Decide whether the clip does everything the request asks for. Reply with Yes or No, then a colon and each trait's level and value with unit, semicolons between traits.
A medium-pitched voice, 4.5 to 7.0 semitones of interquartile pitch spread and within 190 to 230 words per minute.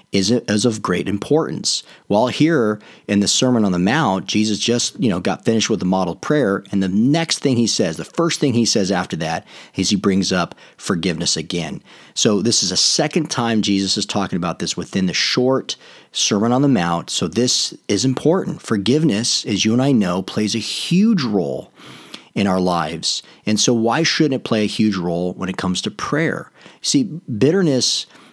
No: low, 110 Hz; average, 5.2 semitones; average, 195 wpm